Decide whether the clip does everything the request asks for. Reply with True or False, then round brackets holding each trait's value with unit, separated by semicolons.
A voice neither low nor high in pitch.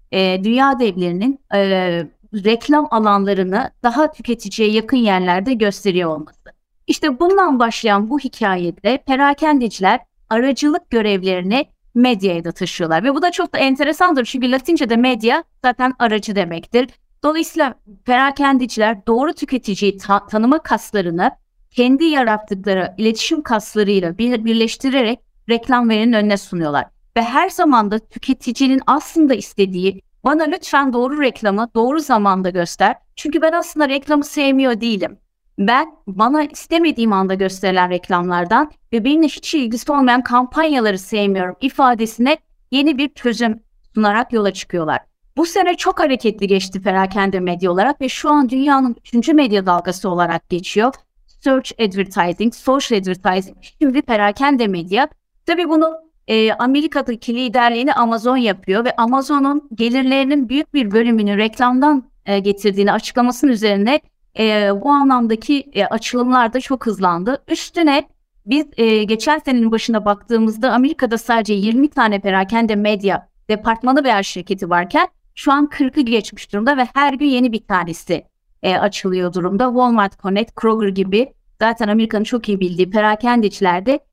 False (235 Hz)